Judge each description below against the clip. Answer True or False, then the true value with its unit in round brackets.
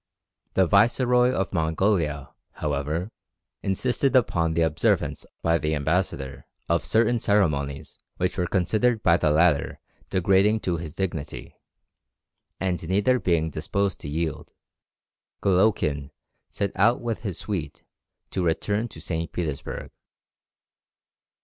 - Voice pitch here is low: True (90 Hz)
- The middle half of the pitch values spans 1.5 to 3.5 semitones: False (4.5 semitones)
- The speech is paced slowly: True (120 wpm)